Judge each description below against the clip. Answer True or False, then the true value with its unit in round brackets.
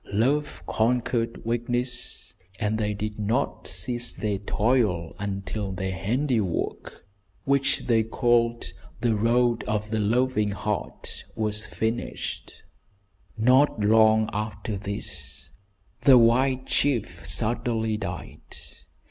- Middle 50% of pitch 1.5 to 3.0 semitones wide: True (2.6 semitones)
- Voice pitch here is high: False (110 Hz)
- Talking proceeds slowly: True (105 wpm)